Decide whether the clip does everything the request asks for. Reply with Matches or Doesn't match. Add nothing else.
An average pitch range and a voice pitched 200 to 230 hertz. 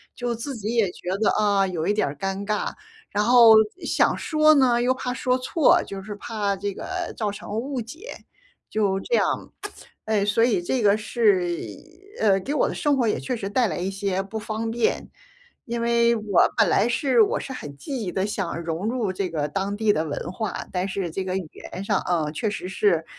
Matches